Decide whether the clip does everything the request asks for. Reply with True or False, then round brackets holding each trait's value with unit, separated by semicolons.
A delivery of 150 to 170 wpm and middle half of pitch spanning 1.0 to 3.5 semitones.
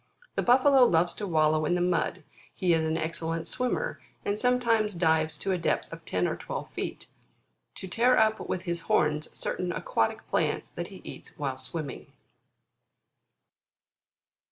False (155 wpm; 5.3 semitones)